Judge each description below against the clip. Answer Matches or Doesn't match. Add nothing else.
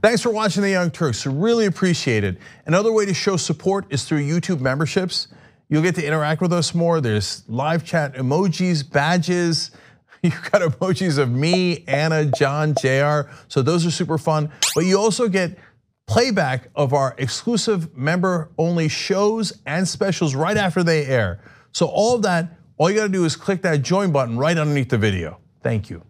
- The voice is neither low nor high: Matches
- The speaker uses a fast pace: Doesn't match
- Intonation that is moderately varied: Matches